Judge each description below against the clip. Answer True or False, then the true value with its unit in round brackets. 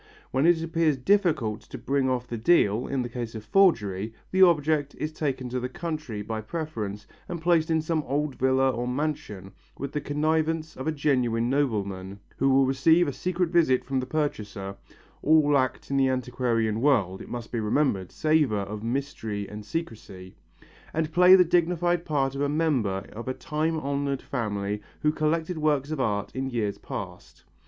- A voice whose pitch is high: False (135 Hz)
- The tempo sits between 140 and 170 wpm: False (180 wpm)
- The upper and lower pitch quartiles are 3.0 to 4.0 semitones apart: False (5.6 semitones)